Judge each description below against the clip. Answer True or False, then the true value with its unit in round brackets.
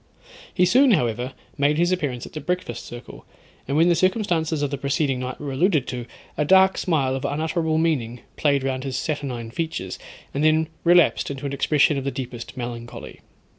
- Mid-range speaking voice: True (145 Hz)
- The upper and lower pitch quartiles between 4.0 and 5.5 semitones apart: True (4.3 semitones)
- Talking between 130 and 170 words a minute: False (185 wpm)